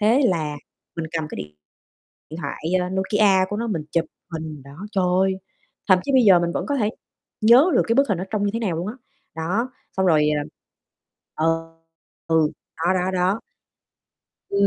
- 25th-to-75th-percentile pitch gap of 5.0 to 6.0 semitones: No, average, 4.3 semitones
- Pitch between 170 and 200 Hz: Yes, medium, 185 Hz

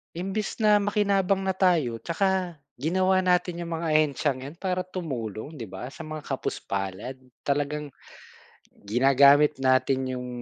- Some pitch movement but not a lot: No, wide, 5.7 semitones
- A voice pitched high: No, medium, 155 Hz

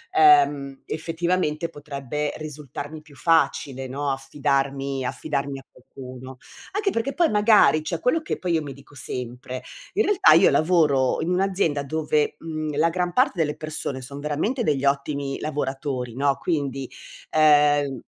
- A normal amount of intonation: Yes, average, 3.3 semitones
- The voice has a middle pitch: Yes, medium, 150 Hz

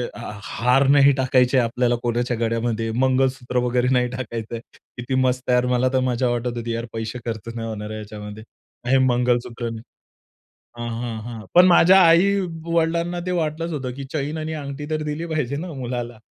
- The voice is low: Yes, low, 125 Hz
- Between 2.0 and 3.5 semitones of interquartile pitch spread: No, average, 3.9 semitones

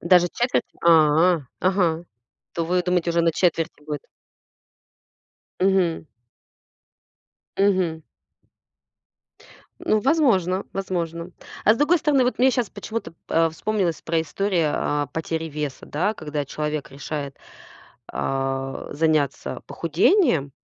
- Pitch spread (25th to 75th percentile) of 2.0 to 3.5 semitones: No, average, 4.1 semitones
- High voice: No, medium, 170 Hz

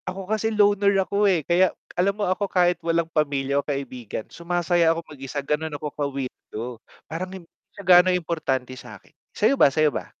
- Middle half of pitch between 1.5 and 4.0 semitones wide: No, average, 4.6 semitones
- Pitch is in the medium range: Yes, medium, 170 Hz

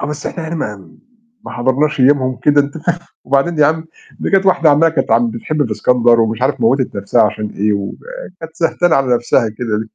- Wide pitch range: Yes, wide, 6.0 semitones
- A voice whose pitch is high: No, medium, 140 Hz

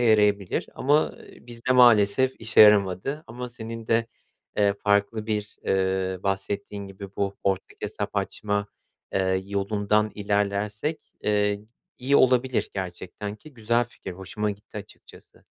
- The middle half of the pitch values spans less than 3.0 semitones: Yes, narrow, 2.5 semitones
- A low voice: Yes, low, 105 Hz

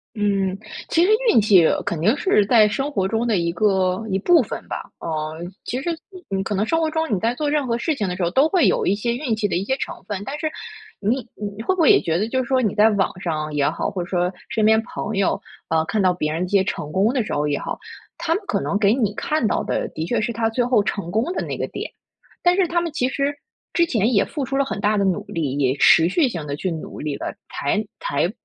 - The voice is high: Yes, high, 210 Hz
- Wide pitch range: Yes, wide, 6.1 semitones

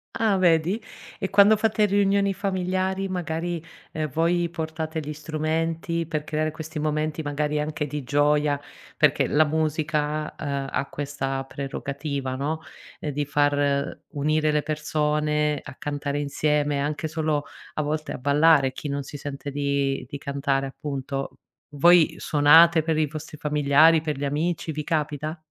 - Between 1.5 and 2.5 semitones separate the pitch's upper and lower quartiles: Yes, narrow, 2.0 semitones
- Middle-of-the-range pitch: Yes, medium, 150 Hz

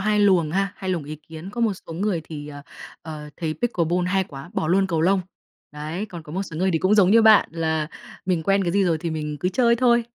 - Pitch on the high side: No, medium, 180 Hz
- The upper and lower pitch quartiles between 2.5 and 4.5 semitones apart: Yes, average, 3.8 semitones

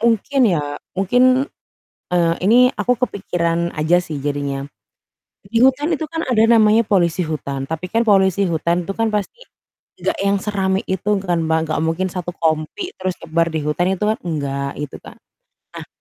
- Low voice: No, medium, 185 Hz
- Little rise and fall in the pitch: No, average, 5.1 semitones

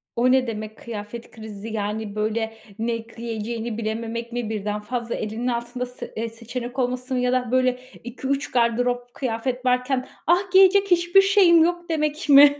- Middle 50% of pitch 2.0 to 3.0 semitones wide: Yes, average, 2.7 semitones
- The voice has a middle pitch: No, high, 245 Hz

